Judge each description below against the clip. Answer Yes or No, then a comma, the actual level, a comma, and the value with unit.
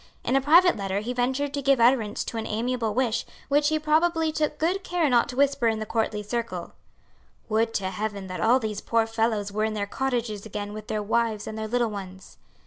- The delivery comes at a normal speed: No, fast, 220 wpm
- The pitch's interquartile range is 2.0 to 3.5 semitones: No, average, 4.2 semitones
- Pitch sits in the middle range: No, high, 230 Hz